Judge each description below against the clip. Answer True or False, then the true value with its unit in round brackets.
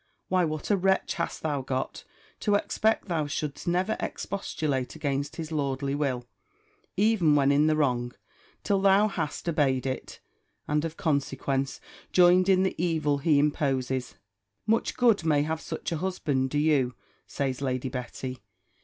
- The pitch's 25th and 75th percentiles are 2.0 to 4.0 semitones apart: False (4.6 semitones)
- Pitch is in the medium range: True (150 Hz)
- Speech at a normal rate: True (150 wpm)